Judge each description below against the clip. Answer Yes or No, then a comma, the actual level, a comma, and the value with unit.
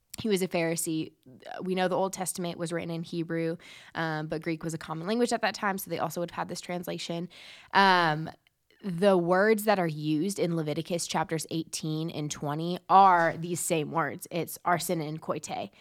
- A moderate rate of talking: Yes, average, 195 wpm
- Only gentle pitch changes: Yes, narrow, 2.2 semitones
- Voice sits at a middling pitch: Yes, medium, 170 Hz